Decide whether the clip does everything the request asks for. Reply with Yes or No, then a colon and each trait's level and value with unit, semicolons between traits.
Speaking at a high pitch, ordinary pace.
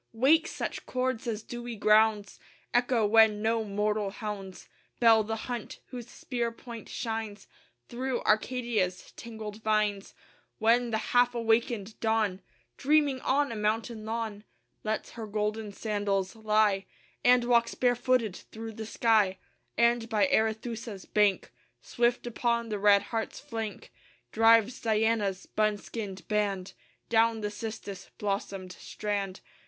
No: high, 220 Hz; slow, 125 wpm